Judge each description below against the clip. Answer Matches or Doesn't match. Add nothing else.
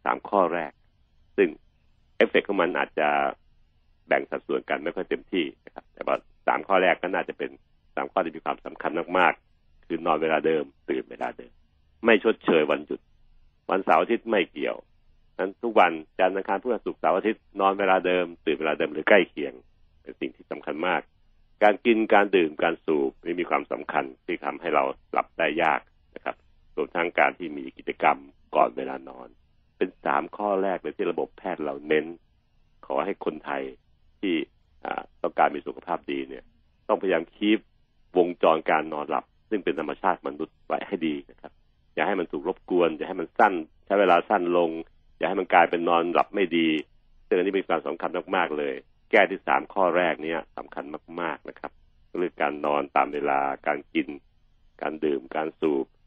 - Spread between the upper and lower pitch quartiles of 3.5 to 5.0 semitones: Matches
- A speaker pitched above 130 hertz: Doesn't match